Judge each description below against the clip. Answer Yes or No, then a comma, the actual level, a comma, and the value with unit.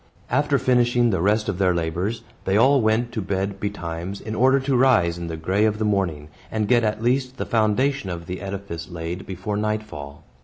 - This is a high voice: No, low, 105 Hz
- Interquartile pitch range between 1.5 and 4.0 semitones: No, average, 4.9 semitones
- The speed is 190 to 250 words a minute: Yes, average, 200 wpm